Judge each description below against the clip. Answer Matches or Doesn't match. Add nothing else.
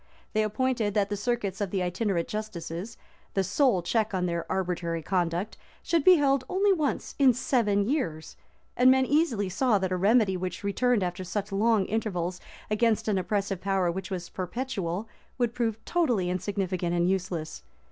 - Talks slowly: Doesn't match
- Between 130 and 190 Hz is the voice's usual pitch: Doesn't match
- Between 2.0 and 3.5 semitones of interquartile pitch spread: Doesn't match